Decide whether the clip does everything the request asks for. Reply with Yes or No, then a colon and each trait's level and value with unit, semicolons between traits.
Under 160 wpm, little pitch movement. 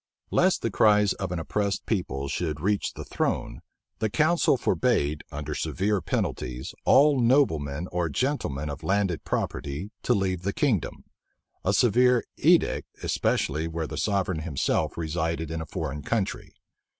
No: average, 145 wpm; wide, 5.6 semitones